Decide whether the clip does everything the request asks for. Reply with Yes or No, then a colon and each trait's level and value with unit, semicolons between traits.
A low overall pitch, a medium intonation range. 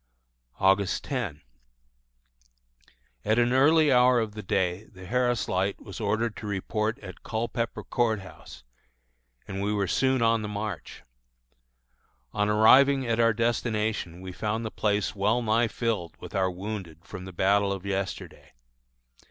Yes: low, 105 Hz; average, 3.2 semitones